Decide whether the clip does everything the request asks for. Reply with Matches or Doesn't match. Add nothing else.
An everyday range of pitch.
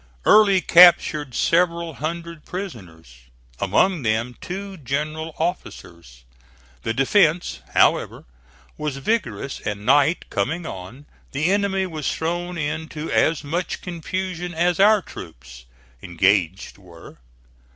Doesn't match